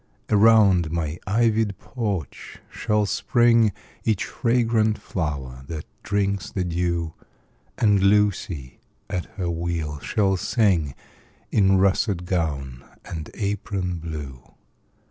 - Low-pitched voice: Yes, very low, 95 Hz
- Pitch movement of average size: Yes, average, 4.3 semitones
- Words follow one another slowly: Yes, slow, 105 wpm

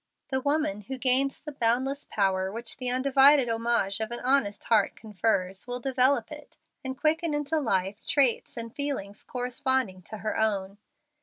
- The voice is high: Yes, high, 245 Hz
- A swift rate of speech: No, average, 165 wpm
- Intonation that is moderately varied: Yes, average, 4.6 semitones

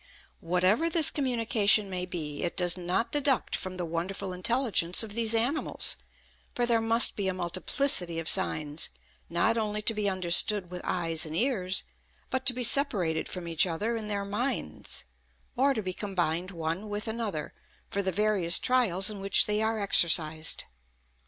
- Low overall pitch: No, high, 195 Hz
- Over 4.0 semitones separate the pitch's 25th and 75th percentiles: Yes, average, 4.6 semitones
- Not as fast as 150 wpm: No, average, 165 wpm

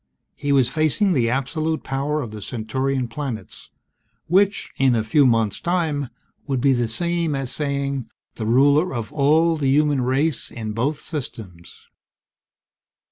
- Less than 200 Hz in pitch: Yes, low, 135 Hz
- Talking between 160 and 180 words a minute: No, average, 145 wpm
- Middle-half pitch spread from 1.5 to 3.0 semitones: No, average, 4.0 semitones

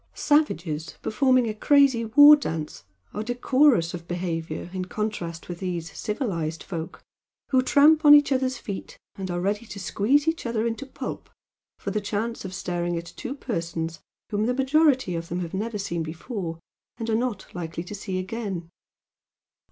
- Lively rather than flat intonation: Yes, wide, 6.7 semitones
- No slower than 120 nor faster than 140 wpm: No, average, 165 wpm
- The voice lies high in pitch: Yes, high, 205 Hz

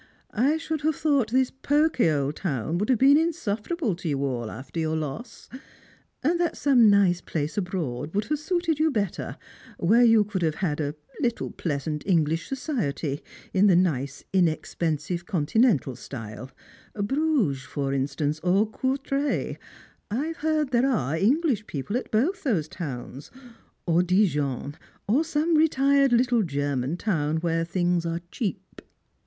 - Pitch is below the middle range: No, high, 190 Hz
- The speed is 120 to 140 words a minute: No, average, 155 wpm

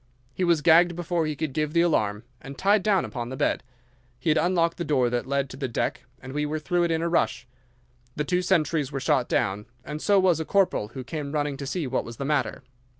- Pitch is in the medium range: Yes, medium, 150 Hz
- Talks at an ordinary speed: No, fast, 245 wpm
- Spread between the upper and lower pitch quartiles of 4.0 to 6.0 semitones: Yes, average, 4.3 semitones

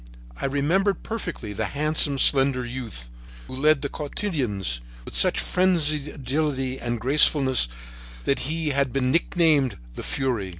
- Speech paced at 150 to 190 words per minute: No, slow, 135 wpm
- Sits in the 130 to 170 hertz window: Yes, medium, 140 Hz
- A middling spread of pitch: Yes, average, 3.3 semitones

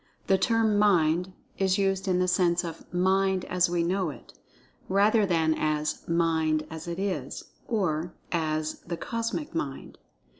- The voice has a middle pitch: Yes, medium, 180 Hz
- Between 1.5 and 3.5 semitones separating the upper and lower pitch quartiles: Yes, average, 3.0 semitones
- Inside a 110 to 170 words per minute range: Yes, average, 145 wpm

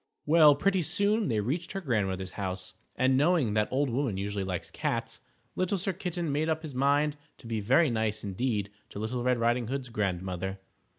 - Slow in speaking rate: No, average, 185 wpm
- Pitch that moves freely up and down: Yes, wide, 7.0 semitones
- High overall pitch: No, low, 125 Hz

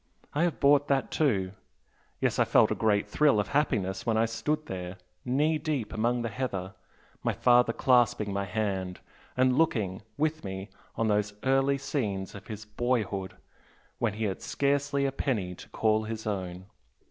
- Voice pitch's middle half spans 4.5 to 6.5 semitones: Yes, wide, 5.5 semitones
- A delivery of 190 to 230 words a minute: No, average, 170 wpm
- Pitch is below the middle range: Yes, low, 110 Hz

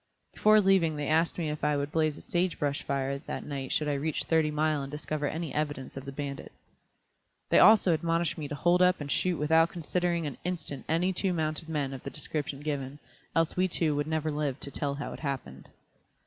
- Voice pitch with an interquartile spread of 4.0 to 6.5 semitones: No, average, 2.7 semitones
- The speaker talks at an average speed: No, fast, 220 wpm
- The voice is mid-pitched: Yes, medium, 155 Hz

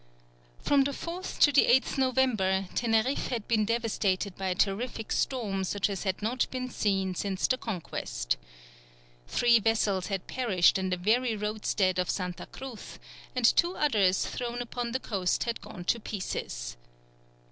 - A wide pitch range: No, average, 4.4 semitones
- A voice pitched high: Yes, high, 215 Hz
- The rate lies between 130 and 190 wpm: Yes, average, 160 wpm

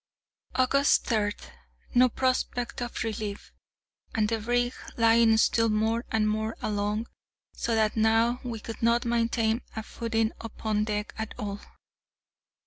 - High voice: Yes, high, 225 Hz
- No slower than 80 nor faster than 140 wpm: Yes, slow, 135 wpm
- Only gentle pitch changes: Yes, narrow, 1.5 semitones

